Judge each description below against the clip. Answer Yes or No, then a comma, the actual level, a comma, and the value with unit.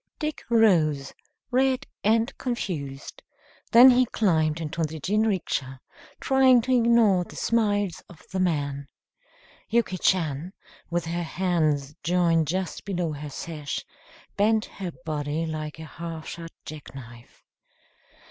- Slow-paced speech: Yes, slow, 125 wpm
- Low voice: No, medium, 170 Hz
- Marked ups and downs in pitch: Yes, wide, 5.9 semitones